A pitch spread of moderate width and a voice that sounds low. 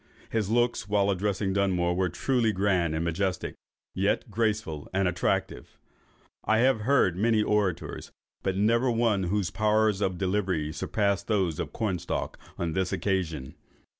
Yes: average, 3.2 semitones; low, 100 Hz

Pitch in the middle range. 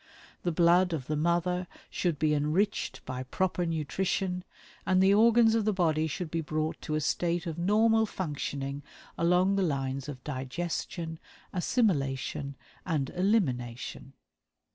Yes: medium, 170 Hz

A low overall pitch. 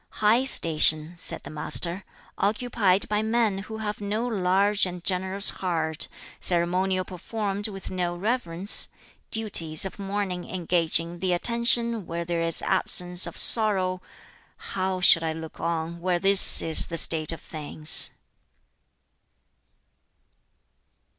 No: medium, 185 Hz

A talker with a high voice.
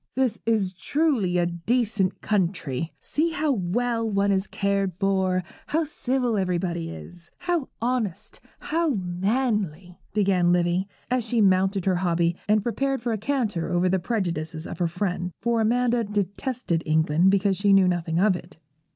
Yes: high, 195 Hz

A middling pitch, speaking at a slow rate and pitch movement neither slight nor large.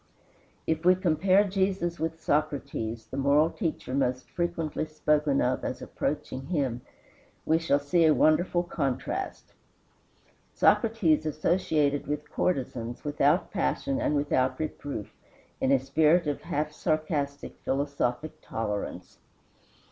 Yes: medium, 150 Hz; slow, 115 wpm; average, 3.3 semitones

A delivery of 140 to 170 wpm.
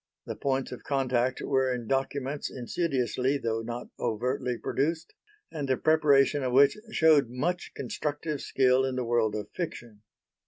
Yes: average, 150 wpm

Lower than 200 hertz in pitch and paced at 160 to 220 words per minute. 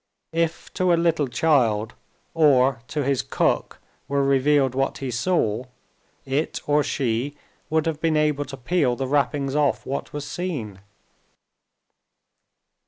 No: medium, 140 Hz; slow, 135 wpm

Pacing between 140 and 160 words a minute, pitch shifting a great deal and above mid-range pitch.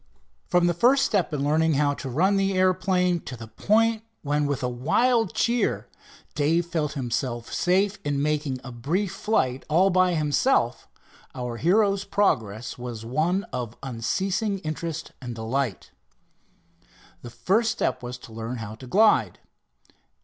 No: average, 150 wpm; wide, 7.4 semitones; medium, 150 Hz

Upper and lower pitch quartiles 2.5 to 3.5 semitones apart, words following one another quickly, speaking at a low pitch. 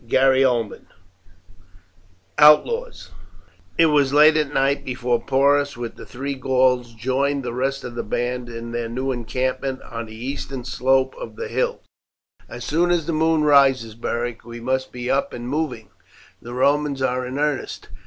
No: average, 2.8 semitones; average, 165 wpm; low, 130 Hz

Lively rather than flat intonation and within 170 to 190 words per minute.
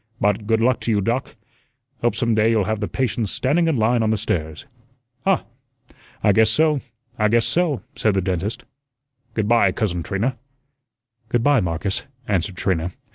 No: average, 3.2 semitones; average, 175 wpm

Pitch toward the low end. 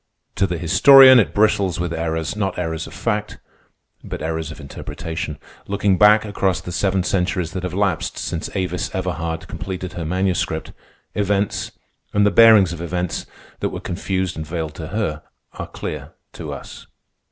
Yes: very low, 90 Hz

